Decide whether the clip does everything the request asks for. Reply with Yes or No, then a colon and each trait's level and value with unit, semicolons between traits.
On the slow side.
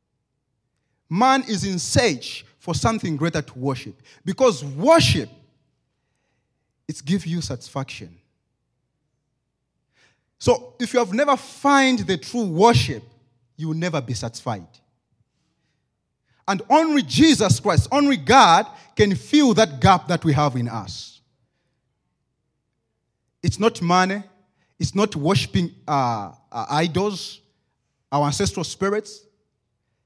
Yes: slow, 110 wpm